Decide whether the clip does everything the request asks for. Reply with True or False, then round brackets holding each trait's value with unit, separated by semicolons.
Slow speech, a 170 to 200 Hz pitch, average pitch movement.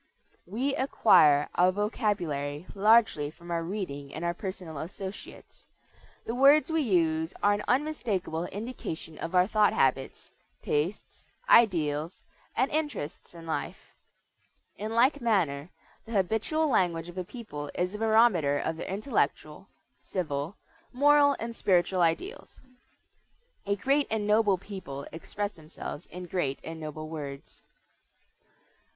False (130 wpm; 185 Hz; 5.7 semitones)